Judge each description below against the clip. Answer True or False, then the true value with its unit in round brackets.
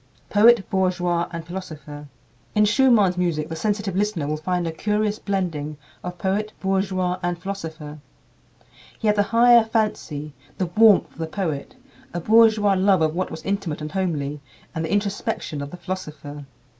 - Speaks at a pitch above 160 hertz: True (185 Hz)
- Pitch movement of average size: True (4.3 semitones)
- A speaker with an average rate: True (160 wpm)